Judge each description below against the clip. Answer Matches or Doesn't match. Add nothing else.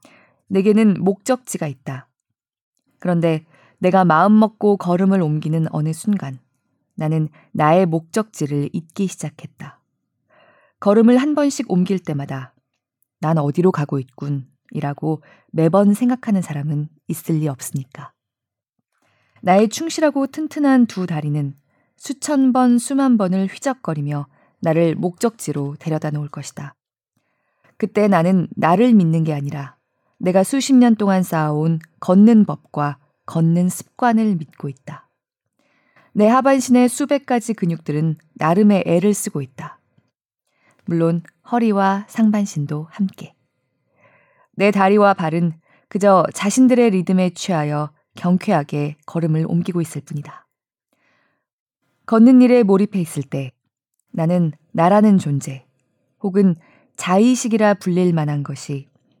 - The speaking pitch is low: Doesn't match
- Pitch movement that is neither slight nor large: Doesn't match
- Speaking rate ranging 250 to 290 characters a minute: Matches